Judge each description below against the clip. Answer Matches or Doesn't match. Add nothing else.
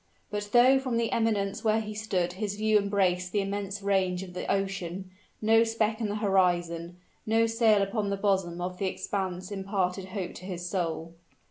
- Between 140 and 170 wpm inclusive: Doesn't match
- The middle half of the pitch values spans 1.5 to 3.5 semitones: Matches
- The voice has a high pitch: Matches